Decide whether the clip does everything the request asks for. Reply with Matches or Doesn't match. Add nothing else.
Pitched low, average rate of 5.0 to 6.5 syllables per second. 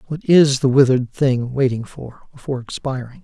Matches